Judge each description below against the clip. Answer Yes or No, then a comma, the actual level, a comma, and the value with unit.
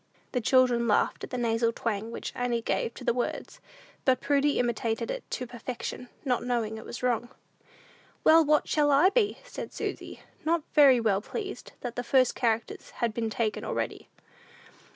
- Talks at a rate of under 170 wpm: No, average, 175 wpm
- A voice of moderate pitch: No, high, 245 Hz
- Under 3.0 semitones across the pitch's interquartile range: No, average, 3.3 semitones